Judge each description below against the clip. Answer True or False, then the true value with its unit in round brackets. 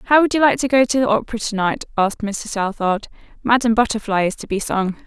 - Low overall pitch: False (225 Hz)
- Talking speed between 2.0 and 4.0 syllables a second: False (6.5 syllables/s)